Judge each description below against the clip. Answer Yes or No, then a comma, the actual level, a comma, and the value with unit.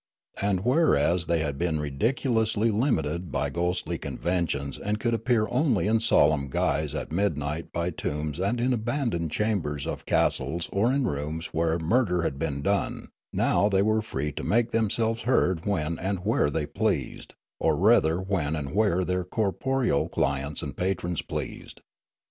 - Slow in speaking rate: No, average, 160 wpm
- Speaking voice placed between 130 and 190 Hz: No, very low, 90 Hz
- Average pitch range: No, wide, 6.1 semitones